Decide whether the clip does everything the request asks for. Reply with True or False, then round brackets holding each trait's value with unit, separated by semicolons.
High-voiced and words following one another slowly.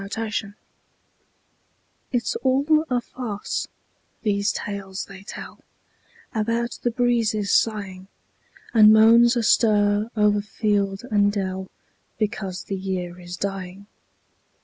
True (210 Hz; 105 wpm)